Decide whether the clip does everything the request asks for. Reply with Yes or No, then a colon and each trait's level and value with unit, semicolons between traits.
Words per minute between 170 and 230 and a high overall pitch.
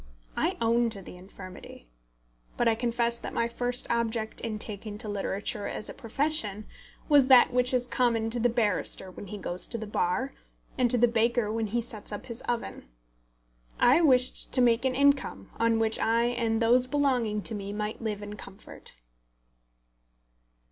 Yes: average, 175 wpm; high, 230 Hz